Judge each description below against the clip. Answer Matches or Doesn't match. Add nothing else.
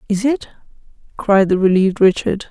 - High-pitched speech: Matches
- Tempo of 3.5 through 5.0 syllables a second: Doesn't match